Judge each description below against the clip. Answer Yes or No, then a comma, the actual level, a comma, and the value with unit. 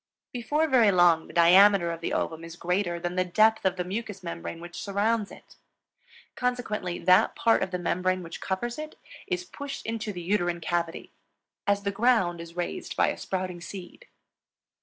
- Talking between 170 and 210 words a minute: Yes, average, 180 wpm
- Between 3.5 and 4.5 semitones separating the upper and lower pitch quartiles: Yes, average, 4.2 semitones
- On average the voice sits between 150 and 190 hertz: Yes, medium, 185 Hz